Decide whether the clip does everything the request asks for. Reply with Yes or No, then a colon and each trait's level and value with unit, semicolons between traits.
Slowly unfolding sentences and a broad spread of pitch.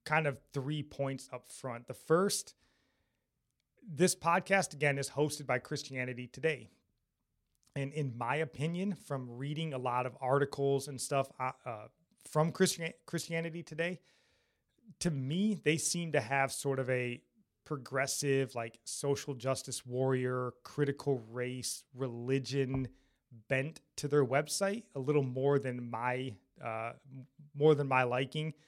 No: slow, 130 wpm; average, 3.1 semitones